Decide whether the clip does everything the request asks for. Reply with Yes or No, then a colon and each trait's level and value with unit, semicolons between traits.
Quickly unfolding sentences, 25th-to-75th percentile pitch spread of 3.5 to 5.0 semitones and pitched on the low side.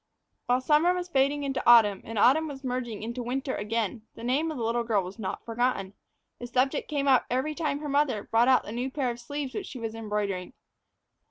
No: fast, 220 wpm; average, 3.8 semitones; very high, 250 Hz